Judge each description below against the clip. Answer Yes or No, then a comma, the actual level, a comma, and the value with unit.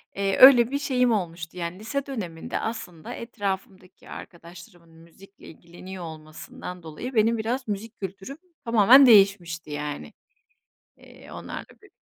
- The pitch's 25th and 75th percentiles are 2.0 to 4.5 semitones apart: No, average, 5.3 semitones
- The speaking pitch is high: Yes, high, 195 Hz